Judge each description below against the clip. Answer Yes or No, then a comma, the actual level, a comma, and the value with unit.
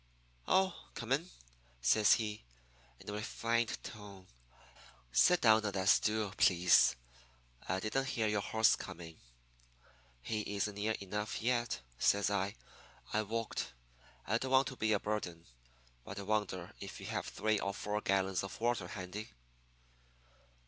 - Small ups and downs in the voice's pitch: Yes, narrow, 2.3 semitones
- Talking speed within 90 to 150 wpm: Yes, average, 145 wpm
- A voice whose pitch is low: Yes, low, 105 Hz